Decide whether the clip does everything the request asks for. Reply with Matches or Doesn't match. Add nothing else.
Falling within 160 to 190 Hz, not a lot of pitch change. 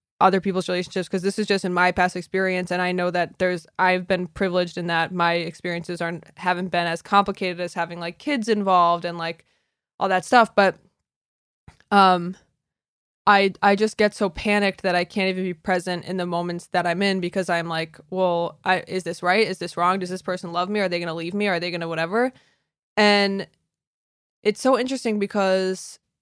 Matches